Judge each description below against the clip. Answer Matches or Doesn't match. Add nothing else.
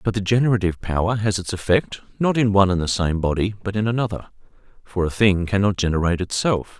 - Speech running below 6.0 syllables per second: Doesn't match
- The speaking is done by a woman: Doesn't match